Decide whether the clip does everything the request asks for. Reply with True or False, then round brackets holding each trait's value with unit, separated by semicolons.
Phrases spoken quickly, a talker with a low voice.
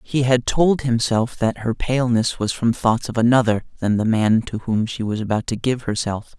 True (215 wpm; 115 Hz)